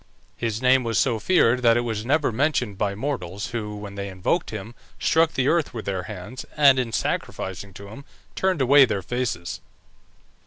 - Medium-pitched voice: No, low, 115 Hz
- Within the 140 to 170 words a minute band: No, average, 185 wpm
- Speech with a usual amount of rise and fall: Yes, average, 4.7 semitones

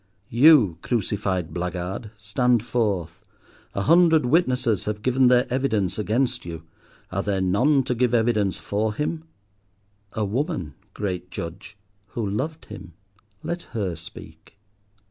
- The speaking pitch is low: Yes, low, 110 Hz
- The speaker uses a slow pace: Yes, slow, 125 wpm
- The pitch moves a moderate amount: Yes, average, 5.0 semitones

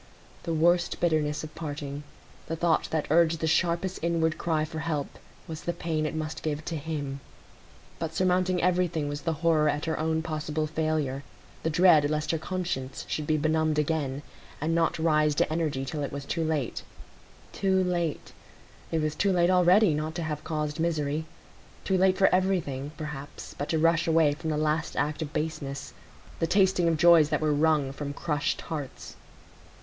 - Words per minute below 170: No, average, 175 wpm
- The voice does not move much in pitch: Yes, narrow, 2.0 semitones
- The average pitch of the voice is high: No, medium, 155 Hz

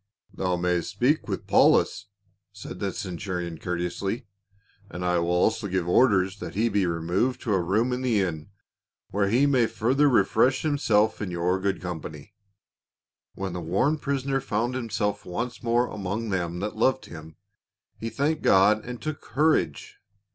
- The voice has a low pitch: Yes, low, 100 Hz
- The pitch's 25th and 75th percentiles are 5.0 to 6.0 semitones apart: Yes, average, 5.3 semitones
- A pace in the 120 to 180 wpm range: Yes, average, 170 wpm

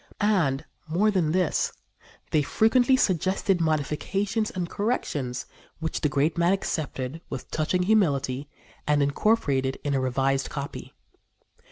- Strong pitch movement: Yes, wide, 5.7 semitones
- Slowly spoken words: Yes, slow, 125 wpm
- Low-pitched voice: No, medium, 155 Hz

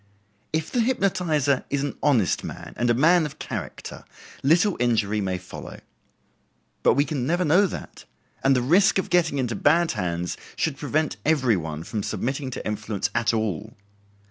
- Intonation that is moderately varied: No, wide, 6.6 semitones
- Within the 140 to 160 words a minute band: No, average, 170 wpm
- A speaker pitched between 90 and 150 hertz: Yes, low, 135 Hz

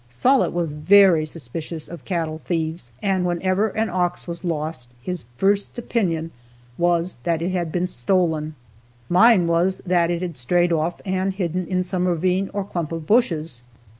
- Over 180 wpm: No, average, 165 wpm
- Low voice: No, medium, 175 Hz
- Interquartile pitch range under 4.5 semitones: Yes, narrow, 2.5 semitones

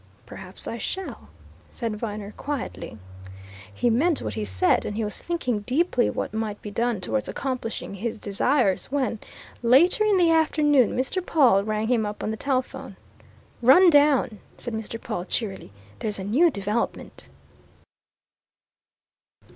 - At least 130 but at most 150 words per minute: Yes, average, 145 wpm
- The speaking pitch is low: No, high, 230 Hz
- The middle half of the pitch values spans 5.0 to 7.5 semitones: Yes, wide, 5.4 semitones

